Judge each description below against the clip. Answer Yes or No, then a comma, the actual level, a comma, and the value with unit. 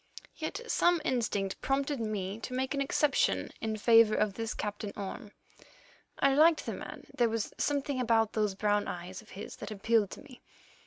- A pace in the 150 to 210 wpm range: Yes, average, 175 wpm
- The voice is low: No, high, 225 Hz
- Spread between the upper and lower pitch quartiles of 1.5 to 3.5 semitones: No, average, 4.2 semitones